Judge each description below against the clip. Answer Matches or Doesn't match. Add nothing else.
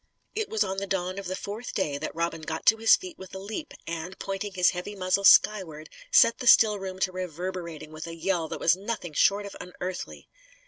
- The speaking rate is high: Matches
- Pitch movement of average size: Matches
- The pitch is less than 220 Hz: Matches